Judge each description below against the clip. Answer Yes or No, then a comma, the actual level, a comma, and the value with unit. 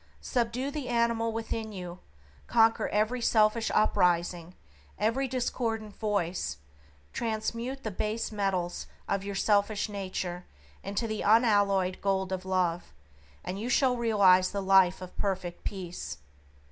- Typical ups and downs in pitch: Yes, average, 3.5 semitones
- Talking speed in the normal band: No, slow, 125 wpm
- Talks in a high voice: Yes, high, 205 Hz